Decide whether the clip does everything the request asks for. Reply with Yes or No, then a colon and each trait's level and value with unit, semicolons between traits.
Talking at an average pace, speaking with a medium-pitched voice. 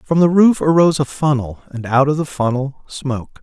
No: fast, 210 wpm; medium, 145 Hz